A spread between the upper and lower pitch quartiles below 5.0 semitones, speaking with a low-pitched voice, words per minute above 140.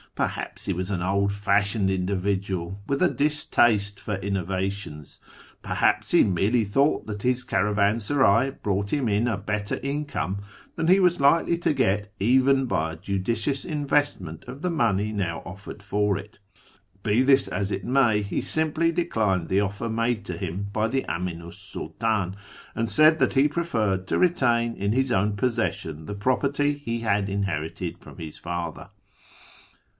No: average, 5.3 semitones; low, 105 Hz; average, 160 wpm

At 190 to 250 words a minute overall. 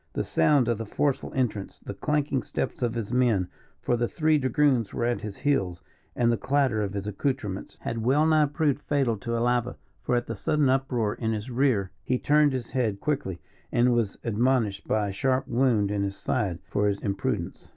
Yes: average, 200 wpm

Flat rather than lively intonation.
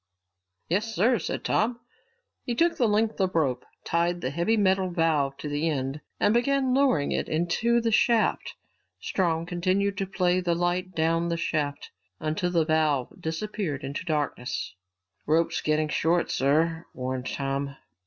No: average, 4.5 semitones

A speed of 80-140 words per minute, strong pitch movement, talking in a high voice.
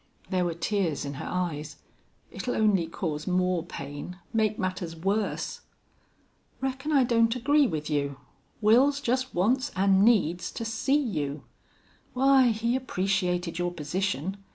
Yes: slow, 135 wpm; wide, 6.0 semitones; high, 195 Hz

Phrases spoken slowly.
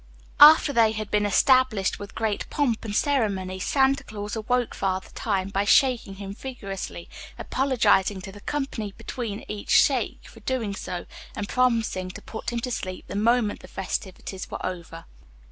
No: average, 160 wpm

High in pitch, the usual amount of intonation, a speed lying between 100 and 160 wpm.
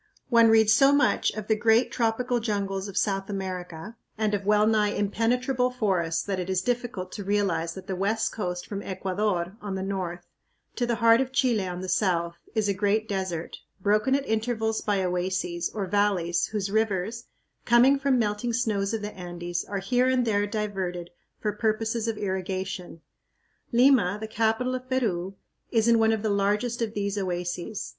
No: high, 205 Hz; average, 3.2 semitones; average, 180 wpm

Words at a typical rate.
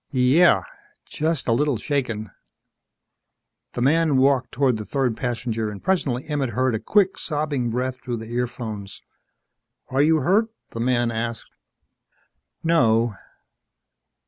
No: slow, 130 wpm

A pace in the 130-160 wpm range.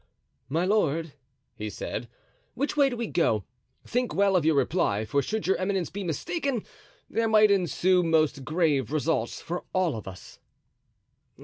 Yes: average, 155 wpm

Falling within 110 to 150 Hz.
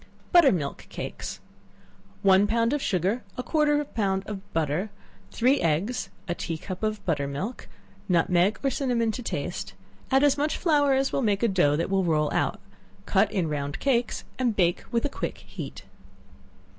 No: high, 210 Hz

